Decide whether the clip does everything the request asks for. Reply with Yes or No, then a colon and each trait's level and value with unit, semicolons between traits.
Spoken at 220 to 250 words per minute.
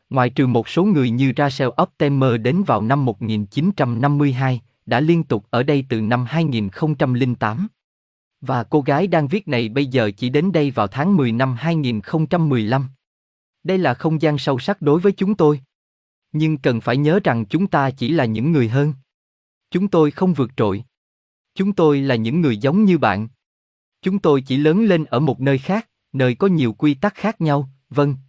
No: average, 185 wpm